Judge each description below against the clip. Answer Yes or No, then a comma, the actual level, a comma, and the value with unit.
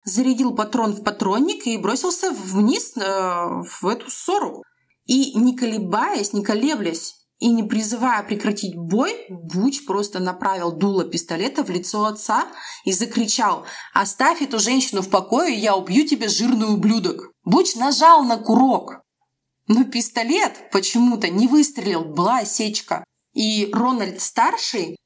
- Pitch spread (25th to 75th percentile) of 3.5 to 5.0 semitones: Yes, average, 4.4 semitones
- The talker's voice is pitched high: Yes, high, 225 Hz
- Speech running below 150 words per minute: Yes, average, 130 wpm